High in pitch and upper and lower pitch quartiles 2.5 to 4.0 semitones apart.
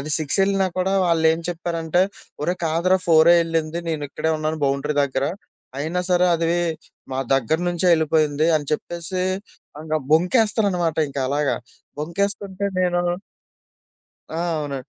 No: medium, 165 Hz; average, 2.9 semitones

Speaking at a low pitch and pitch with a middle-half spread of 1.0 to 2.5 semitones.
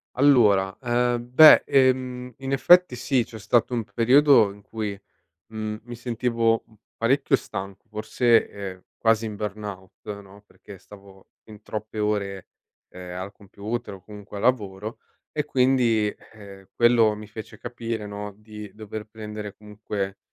No: low, 110 Hz; average, 2.9 semitones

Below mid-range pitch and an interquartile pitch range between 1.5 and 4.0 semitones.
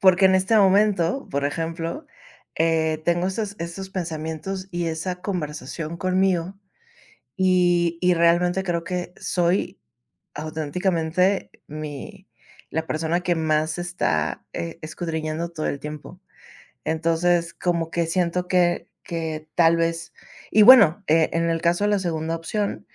No: medium, 170 Hz; narrow, 2.4 semitones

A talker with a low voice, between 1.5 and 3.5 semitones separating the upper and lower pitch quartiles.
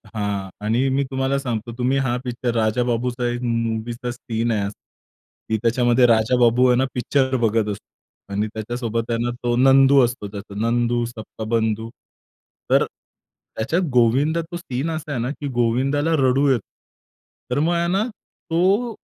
Yes: low, 120 Hz; average, 2.8 semitones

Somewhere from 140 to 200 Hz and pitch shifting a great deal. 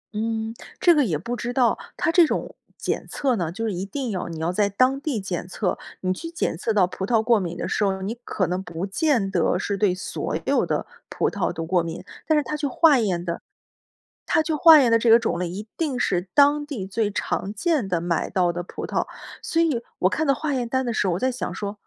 No: high, 220 Hz; wide, 6.6 semitones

